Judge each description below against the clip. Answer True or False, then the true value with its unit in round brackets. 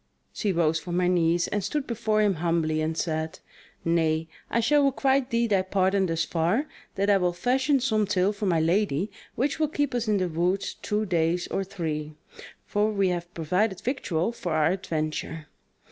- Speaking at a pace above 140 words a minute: True (185 wpm)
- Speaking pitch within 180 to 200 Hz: True (185 Hz)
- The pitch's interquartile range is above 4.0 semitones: True (4.6 semitones)